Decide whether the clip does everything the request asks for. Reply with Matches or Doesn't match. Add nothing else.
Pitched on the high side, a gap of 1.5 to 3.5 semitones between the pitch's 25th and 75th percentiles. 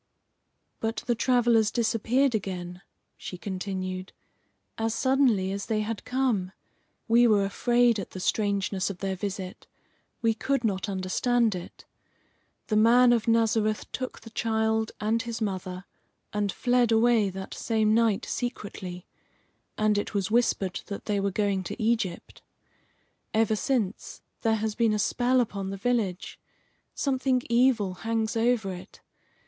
Matches